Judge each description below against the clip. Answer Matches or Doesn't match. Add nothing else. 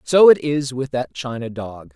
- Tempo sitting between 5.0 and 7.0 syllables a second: Doesn't match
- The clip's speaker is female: Doesn't match